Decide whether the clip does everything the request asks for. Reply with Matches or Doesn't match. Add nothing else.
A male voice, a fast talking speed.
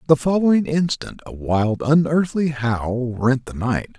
Doesn't match